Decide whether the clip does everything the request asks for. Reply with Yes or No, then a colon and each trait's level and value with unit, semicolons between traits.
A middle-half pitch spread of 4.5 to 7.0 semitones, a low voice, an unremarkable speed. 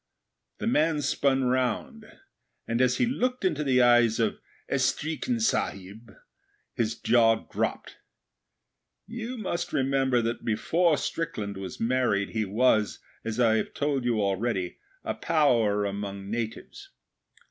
No: average, 5.3 semitones; low, 120 Hz; slow, 125 wpm